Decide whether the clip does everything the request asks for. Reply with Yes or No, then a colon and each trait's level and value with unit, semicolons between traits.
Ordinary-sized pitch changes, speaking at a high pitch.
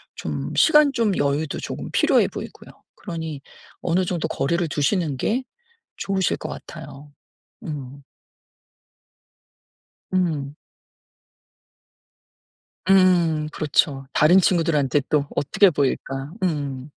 No: average, 4.3 semitones; medium, 155 Hz